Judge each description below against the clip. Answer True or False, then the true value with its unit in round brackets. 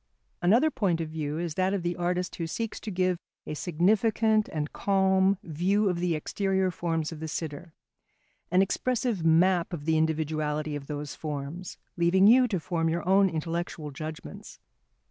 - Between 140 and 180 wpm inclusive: True (170 wpm)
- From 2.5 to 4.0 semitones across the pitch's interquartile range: True (3.3 semitones)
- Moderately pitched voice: True (175 Hz)